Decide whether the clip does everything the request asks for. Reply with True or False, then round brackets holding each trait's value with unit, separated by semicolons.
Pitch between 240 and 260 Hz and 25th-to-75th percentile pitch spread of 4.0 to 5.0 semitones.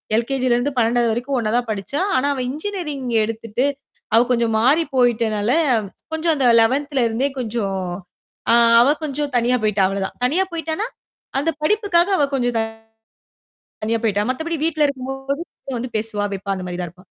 True (250 Hz; 4.4 semitones)